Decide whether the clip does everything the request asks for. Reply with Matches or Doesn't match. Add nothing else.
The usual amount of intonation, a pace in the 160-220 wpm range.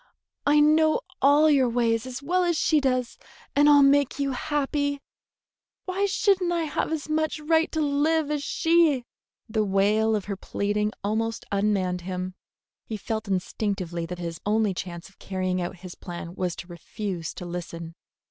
Doesn't match